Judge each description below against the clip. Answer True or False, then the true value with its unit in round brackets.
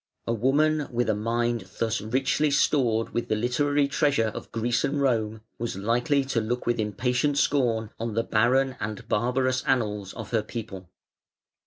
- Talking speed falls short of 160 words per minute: False (165 wpm)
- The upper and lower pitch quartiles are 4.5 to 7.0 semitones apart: False (3.4 semitones)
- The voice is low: True (120 Hz)